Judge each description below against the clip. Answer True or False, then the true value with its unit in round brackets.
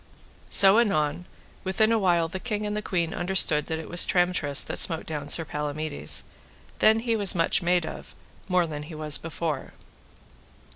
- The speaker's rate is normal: True (175 wpm)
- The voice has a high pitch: False (170 Hz)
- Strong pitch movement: False (3.7 semitones)